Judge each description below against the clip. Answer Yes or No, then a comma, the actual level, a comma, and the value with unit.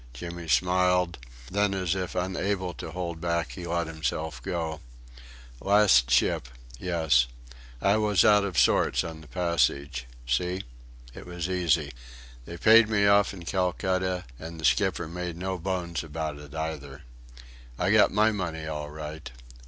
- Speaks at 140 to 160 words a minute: Yes, average, 150 wpm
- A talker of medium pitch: No, very low, 85 Hz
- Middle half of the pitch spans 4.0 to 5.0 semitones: No, average, 2.9 semitones